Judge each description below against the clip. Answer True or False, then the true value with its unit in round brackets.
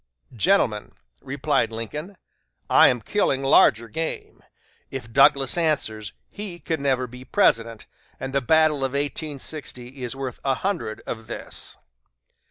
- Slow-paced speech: True (130 wpm)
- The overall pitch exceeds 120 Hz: True (135 Hz)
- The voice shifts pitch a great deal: False (4.2 semitones)